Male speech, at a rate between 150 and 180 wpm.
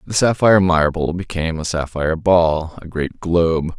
Yes: male; average, 160 wpm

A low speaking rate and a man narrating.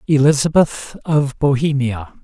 Yes: slow, 80 wpm; male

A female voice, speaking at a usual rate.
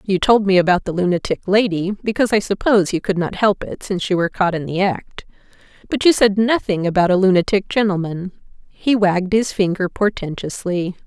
Yes: female; average, 180 wpm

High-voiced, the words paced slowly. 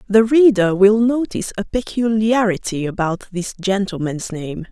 Yes: high, 205 Hz; slow, 125 wpm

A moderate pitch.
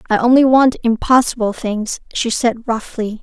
No: high, 235 Hz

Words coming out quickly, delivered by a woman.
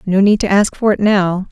Yes: fast, 275 wpm; female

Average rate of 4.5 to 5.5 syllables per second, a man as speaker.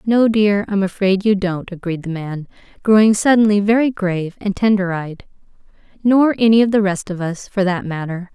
No: 5.1 syllables/s; female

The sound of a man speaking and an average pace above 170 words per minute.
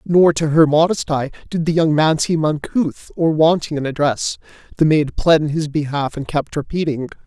Yes: male; average, 200 wpm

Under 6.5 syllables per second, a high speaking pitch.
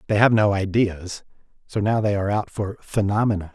No: 5.5 syllables/s; low, 100 Hz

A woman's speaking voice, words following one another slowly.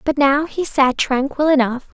No: female; average, 180 wpm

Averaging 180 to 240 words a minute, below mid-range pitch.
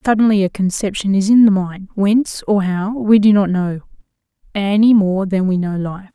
No: average, 195 wpm; high, 200 Hz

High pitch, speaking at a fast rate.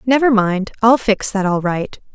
No: high, 215 Hz; average, 195 wpm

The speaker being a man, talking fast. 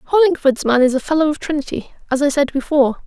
No: female; fast, 215 wpm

